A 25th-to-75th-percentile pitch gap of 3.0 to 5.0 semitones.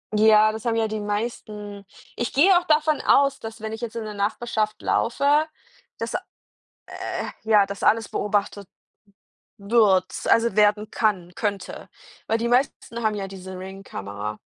No: narrow, 2.5 semitones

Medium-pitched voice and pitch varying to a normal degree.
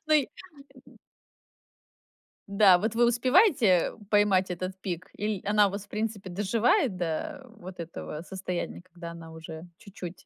No: high, 195 Hz; average, 3.9 semitones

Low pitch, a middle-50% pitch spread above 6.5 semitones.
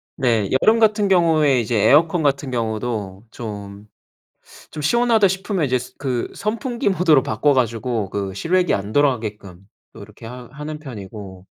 Yes: low, 130 Hz; wide, 7.5 semitones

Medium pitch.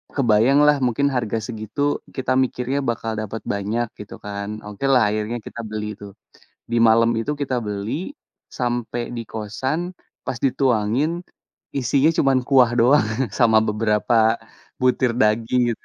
No: low, 120 Hz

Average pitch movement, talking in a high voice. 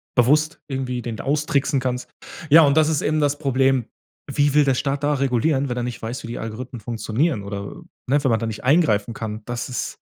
No: average, 3.6 semitones; low, 130 Hz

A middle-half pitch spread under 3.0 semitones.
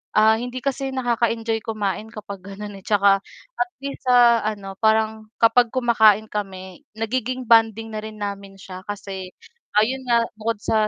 Yes: narrow, 2.5 semitones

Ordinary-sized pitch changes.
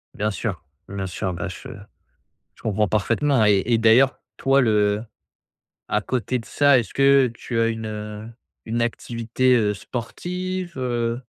Yes: average, 3.4 semitones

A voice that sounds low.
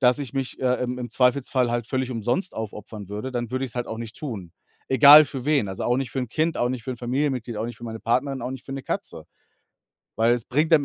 Yes: low, 125 Hz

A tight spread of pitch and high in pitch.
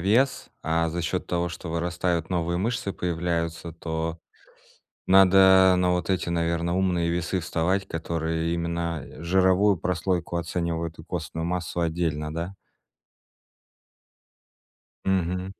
No: narrow, 1.8 semitones; very low, 85 Hz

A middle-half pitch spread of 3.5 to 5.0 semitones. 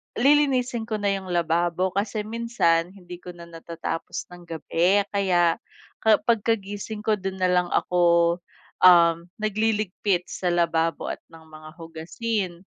Yes: average, 3.8 semitones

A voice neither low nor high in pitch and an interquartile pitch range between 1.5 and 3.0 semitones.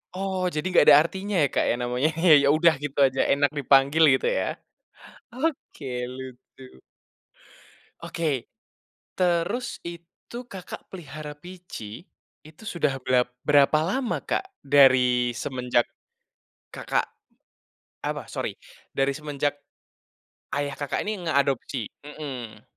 No: medium, 145 Hz; average, 4.7 semitones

